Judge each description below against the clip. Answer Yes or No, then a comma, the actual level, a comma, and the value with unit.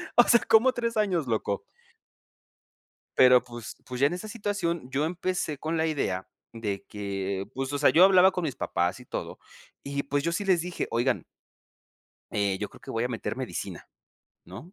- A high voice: No, medium, 140 Hz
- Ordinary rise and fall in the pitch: No, wide, 7.9 semitones